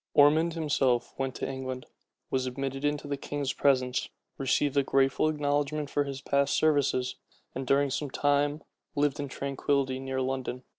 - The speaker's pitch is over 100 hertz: Yes, medium, 140 Hz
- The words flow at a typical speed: Yes, average, 160 wpm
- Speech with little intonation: Yes, narrow, 1.6 semitones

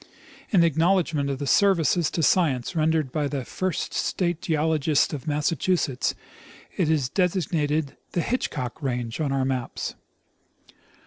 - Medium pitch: Yes, medium, 155 Hz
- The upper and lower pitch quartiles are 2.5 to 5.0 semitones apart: Yes, average, 3.6 semitones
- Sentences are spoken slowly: Yes, slow, 130 wpm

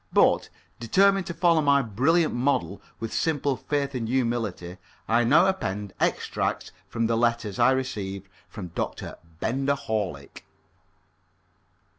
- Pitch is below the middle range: Yes, low, 120 Hz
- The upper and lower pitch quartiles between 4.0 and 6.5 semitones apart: Yes, average, 5.1 semitones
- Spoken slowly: Yes, slow, 125 wpm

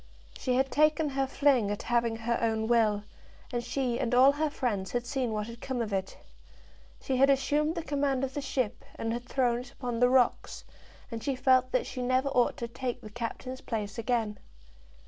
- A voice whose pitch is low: No, high, 245 Hz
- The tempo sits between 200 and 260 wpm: Yes, fast, 205 wpm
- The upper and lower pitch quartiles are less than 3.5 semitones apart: Yes, narrow, 2.6 semitones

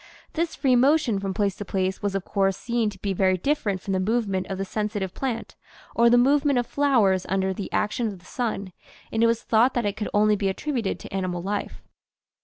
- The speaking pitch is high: Yes, high, 210 Hz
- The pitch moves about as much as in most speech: Yes, average, 3.8 semitones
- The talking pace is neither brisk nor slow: No, fast, 220 wpm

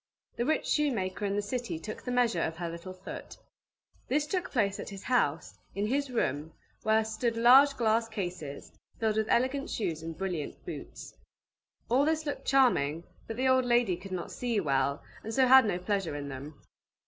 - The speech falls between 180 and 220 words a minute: Yes, average, 185 wpm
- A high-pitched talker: Yes, high, 215 Hz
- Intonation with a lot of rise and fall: Yes, wide, 6.5 semitones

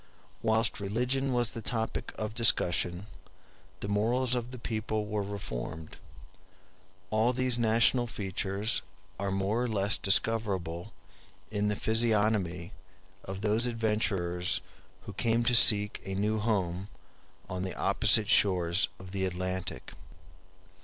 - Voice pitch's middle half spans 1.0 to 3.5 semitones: Yes, average, 3.0 semitones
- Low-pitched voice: Yes, low, 105 Hz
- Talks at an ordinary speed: No, slow, 125 wpm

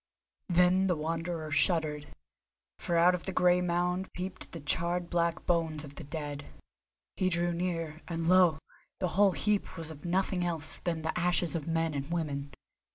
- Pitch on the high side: No, medium, 170 Hz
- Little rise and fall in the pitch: Yes, narrow, 2.0 semitones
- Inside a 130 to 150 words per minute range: No, average, 170 wpm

